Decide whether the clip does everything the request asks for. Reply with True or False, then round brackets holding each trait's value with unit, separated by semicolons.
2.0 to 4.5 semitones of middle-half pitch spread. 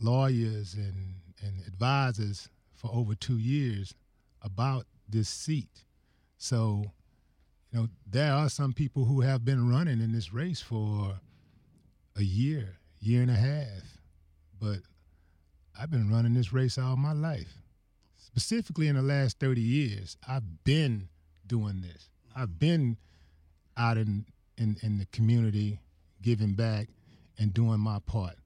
False (5.2 semitones)